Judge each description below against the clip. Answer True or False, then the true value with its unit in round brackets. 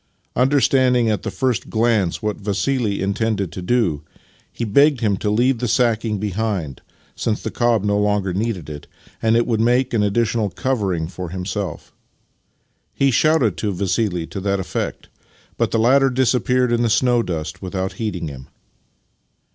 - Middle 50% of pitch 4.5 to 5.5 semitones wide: False (3.9 semitones)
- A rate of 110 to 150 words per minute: False (165 wpm)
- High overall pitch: False (110 Hz)